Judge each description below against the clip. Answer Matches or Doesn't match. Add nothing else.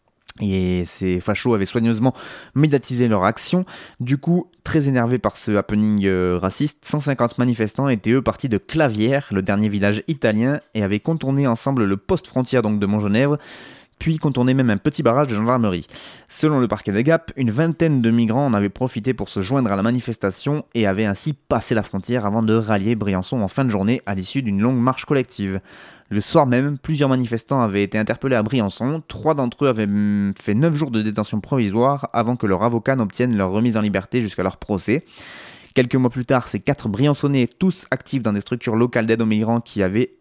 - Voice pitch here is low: Matches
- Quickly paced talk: Doesn't match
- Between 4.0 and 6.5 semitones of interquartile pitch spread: Matches